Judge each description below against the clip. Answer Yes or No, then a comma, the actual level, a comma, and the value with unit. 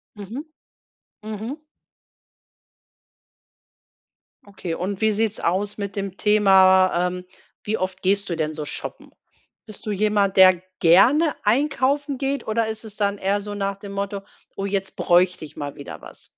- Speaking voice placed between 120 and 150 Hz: No, high, 200 Hz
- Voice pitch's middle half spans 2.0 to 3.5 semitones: Yes, narrow, 2.5 semitones